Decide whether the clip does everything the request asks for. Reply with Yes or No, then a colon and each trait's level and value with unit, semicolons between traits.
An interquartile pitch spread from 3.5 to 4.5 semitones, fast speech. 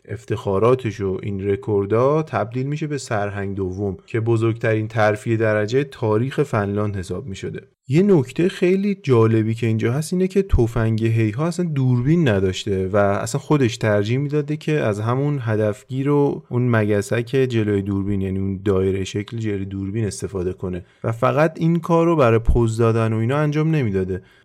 No: wide, 5.6 semitones; fast, 160 wpm